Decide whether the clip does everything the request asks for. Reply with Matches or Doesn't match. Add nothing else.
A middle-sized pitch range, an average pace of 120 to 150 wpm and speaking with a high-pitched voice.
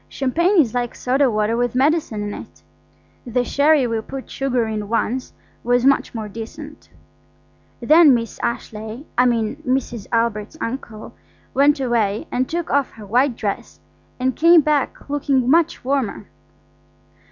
Matches